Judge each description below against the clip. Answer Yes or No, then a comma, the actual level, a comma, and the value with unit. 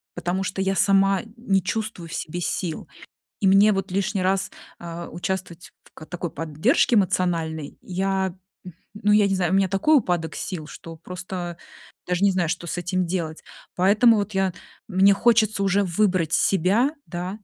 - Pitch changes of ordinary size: No, narrow, 2.3 semitones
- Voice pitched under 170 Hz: No, high, 190 Hz